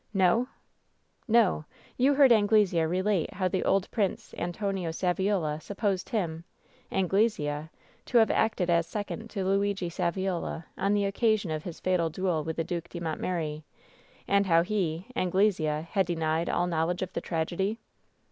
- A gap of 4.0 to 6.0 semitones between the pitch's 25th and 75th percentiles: No, average, 3.5 semitones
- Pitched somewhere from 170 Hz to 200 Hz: Yes, medium, 185 Hz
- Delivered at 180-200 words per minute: No, average, 165 wpm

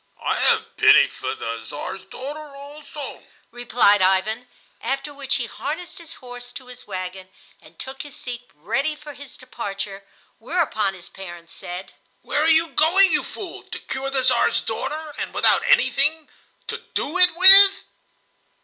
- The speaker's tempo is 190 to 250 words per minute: No, average, 155 wpm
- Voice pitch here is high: Yes, very high, 270 Hz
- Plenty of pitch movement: Yes, wide, 7.4 semitones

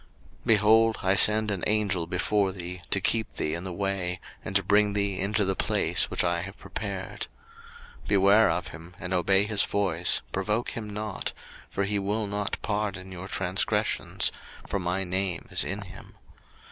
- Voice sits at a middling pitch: No, low, 100 Hz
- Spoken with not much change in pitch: Yes, narrow, 2.3 semitones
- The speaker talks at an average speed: Yes, average, 175 wpm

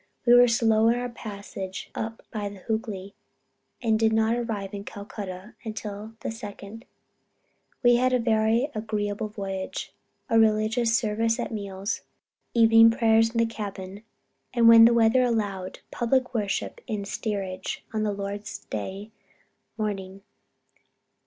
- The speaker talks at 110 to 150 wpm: Yes, slow, 135 wpm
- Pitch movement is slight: Yes, narrow, 2.1 semitones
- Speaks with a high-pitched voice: Yes, high, 220 Hz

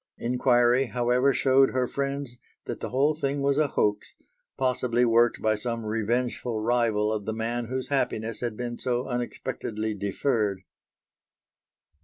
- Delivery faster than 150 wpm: No, average, 140 wpm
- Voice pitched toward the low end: Yes, low, 120 Hz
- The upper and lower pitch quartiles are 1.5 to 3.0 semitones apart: Yes, average, 2.7 semitones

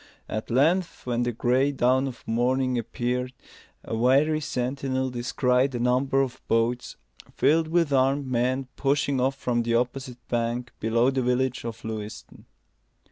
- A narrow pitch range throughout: Yes, narrow, 2.0 semitones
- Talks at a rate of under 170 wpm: Yes, average, 145 wpm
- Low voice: Yes, low, 125 Hz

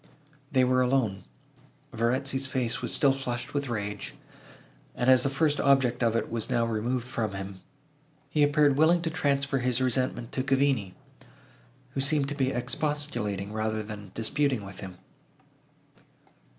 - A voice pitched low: Yes, low, 130 Hz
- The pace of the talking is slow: No, average, 150 wpm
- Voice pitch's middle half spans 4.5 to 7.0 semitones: No, average, 3.8 semitones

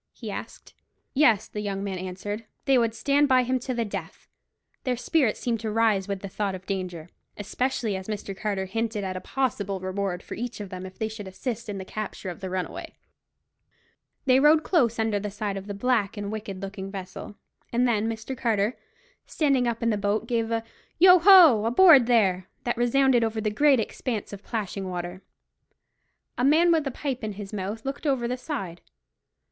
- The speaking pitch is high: Yes, high, 220 Hz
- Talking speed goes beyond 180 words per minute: Yes, average, 195 wpm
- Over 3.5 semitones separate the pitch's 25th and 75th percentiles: Yes, average, 4.1 semitones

